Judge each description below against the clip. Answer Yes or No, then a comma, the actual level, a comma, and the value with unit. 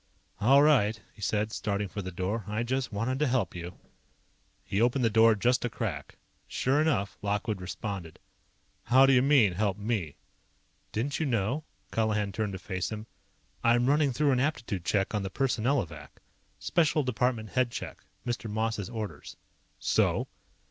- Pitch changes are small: No, average, 4.1 semitones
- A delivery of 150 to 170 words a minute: Yes, average, 160 wpm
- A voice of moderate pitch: No, low, 110 Hz